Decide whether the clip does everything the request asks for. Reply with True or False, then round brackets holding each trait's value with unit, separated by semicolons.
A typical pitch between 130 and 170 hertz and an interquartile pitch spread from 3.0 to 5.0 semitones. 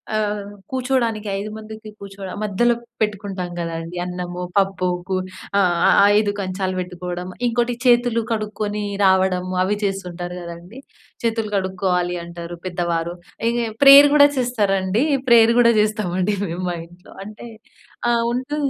False (200 Hz; 3.9 semitones)